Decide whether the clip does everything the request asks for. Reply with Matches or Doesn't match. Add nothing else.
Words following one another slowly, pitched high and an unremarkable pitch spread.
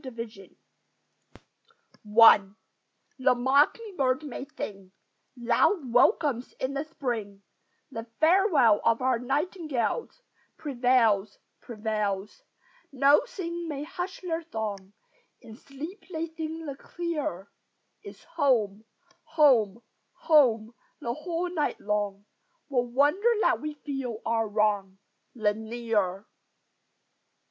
Doesn't match